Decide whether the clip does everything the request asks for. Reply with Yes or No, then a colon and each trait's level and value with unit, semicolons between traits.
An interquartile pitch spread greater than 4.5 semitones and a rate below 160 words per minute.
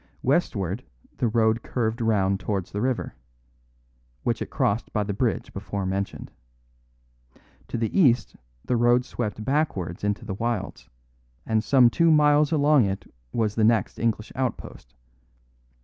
No: average, 3.7 semitones; average, 140 wpm